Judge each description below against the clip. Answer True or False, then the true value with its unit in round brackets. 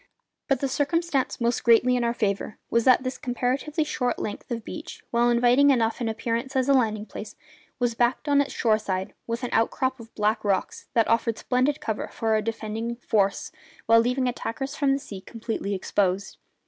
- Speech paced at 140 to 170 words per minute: False (190 wpm)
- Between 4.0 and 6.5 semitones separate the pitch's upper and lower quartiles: False (2.8 semitones)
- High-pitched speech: True (235 Hz)